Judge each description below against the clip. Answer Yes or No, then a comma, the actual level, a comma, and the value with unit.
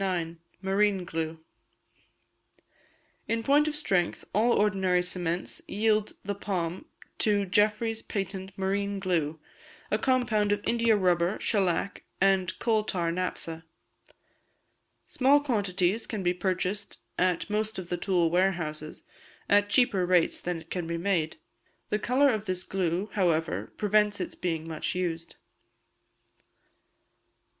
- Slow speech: Yes, slow, 125 wpm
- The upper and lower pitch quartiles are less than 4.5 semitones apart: Yes, average, 3.1 semitones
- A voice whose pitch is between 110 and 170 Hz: No, high, 190 Hz